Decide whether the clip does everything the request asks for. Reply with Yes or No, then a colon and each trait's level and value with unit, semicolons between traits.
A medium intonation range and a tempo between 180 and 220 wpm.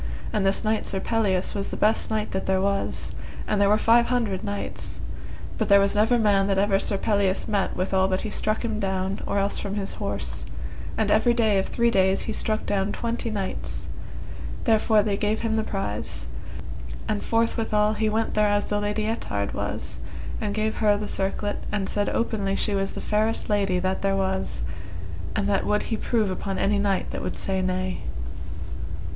No: narrow, 1.9 semitones; average, 190 wpm